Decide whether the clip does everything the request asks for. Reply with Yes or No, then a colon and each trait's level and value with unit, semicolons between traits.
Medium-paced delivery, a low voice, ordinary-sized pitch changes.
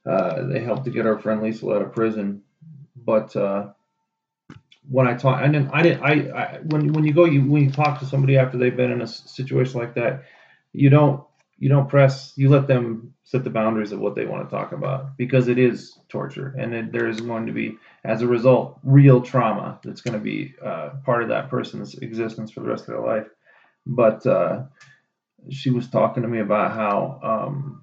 No: fast, 220 wpm; low, 130 Hz; average, 3.4 semitones